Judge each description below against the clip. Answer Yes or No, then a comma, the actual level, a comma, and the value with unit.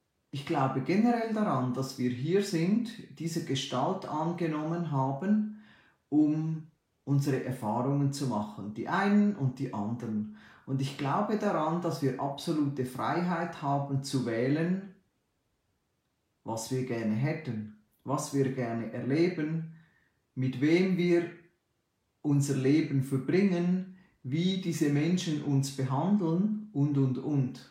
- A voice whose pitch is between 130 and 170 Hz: Yes, medium, 140 Hz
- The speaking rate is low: Yes, slow, 120 wpm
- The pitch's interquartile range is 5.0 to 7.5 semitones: No, average, 4.6 semitones